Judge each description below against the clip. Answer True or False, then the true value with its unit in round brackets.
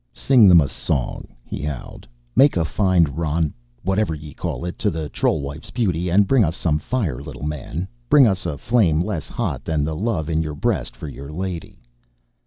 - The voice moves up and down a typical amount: True (4.2 semitones)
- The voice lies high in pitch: False (80 Hz)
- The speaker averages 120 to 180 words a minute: False (195 wpm)